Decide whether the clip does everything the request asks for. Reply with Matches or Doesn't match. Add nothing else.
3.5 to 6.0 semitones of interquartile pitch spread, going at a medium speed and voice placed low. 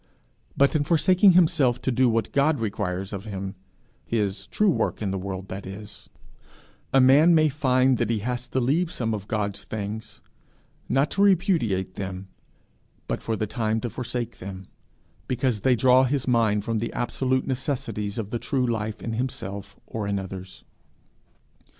Matches